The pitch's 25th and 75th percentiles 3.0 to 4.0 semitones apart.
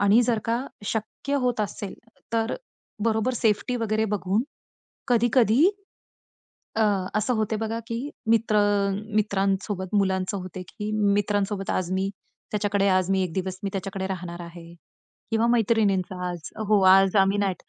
No: narrow, 2.6 semitones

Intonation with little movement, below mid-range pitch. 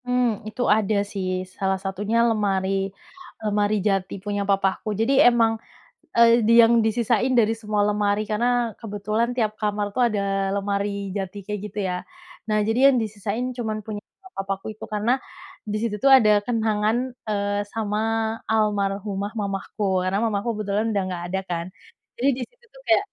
No: narrow, 2.2 semitones; high, 210 Hz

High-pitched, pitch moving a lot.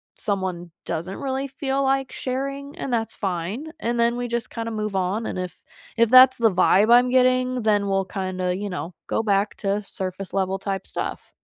No: high, 215 Hz; average, 4.9 semitones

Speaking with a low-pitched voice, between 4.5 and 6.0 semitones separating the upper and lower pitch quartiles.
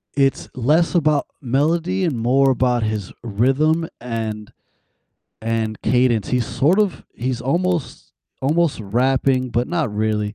Yes: low, 130 Hz; average, 5.2 semitones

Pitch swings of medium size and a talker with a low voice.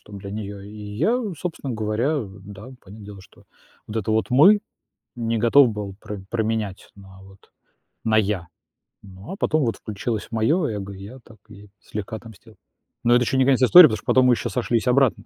Yes: average, 3.6 semitones; low, 110 Hz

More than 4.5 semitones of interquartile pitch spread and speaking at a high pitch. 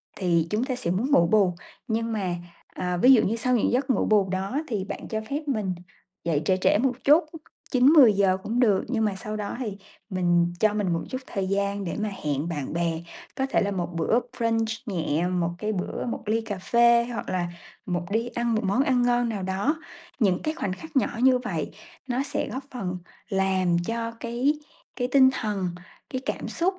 Yes: average, 4.9 semitones; high, 215 Hz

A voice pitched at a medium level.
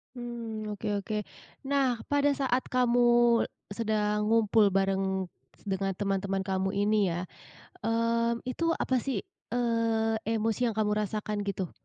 No: high, 215 Hz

